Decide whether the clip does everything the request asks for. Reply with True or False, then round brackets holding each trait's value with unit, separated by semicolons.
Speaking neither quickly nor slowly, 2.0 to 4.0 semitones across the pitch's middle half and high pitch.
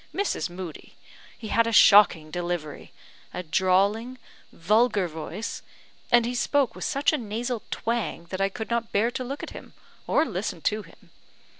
False (165 wpm; 4.6 semitones; 215 Hz)